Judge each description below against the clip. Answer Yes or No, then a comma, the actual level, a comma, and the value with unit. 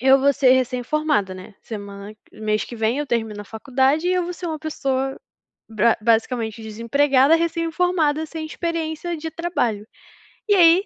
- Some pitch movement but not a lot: No, wide, 6.3 semitones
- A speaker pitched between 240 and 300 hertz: Yes, very high, 270 Hz